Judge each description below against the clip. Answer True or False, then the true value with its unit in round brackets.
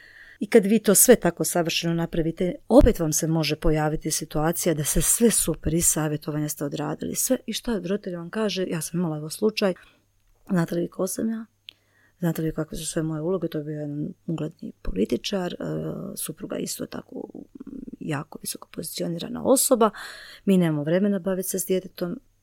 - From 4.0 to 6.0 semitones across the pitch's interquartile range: True (4.3 semitones)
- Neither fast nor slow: False (185 wpm)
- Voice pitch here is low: False (170 Hz)